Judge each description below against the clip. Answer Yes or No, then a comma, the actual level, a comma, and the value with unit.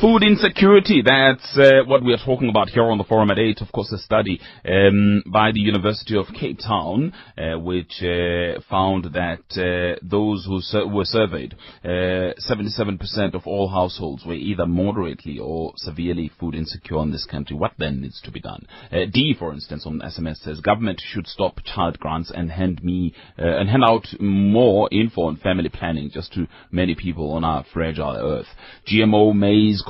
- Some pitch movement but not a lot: Yes, average, 4.1 semitones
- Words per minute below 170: No, average, 185 wpm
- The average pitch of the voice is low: Yes, very low, 95 Hz